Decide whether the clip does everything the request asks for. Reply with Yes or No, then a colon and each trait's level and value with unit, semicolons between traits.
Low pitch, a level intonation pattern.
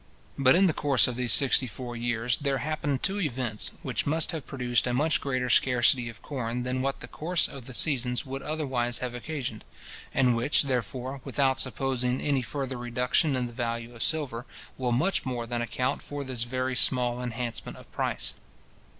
Yes: low, 130 Hz; narrow, 2.3 semitones